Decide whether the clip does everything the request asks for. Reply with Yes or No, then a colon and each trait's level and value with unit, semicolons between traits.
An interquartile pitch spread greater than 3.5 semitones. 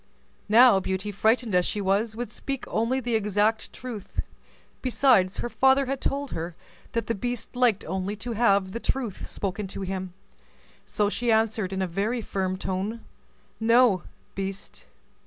Yes: average, 3.9 semitones